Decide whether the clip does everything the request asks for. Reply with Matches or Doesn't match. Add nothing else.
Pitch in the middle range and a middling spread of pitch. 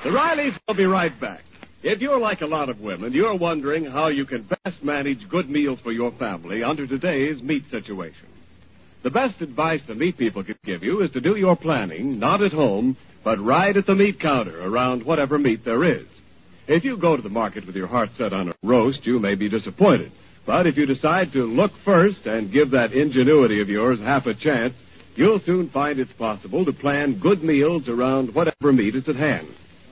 Doesn't match